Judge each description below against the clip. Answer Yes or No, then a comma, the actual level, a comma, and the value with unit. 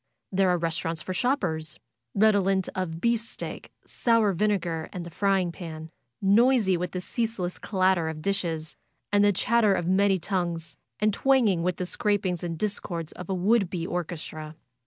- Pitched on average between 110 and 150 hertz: No, medium, 185 Hz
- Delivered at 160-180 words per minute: Yes, average, 165 wpm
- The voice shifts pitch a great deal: No, average, 3.3 semitones